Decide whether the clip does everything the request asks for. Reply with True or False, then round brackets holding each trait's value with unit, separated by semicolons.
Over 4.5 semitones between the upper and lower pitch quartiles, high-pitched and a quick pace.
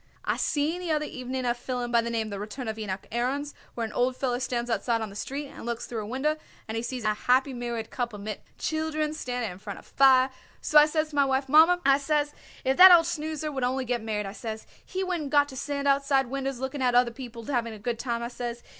False (3.5 semitones; 255 Hz; 255 wpm)